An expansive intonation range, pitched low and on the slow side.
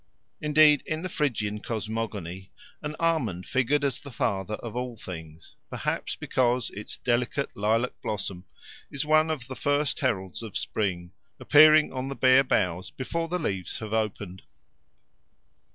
No: wide, 6.1 semitones; low, 120 Hz; average, 150 wpm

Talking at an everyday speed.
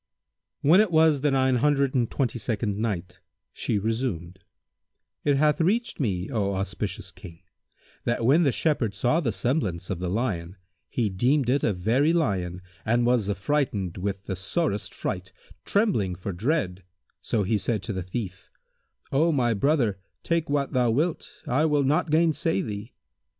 Yes: average, 160 wpm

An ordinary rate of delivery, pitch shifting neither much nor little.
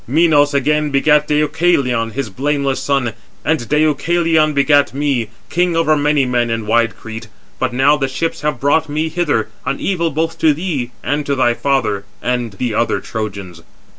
Yes: average, 165 wpm; average, 4.0 semitones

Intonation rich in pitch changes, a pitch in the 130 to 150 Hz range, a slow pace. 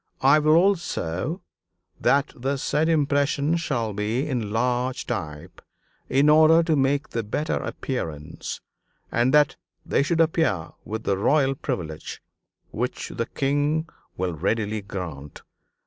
Yes: wide, 6.4 semitones; low, 135 Hz; slow, 130 wpm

